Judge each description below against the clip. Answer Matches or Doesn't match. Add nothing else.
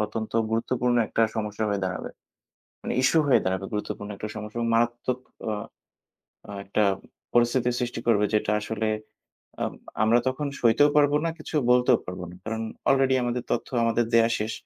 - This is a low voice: Matches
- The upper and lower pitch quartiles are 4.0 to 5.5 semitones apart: Doesn't match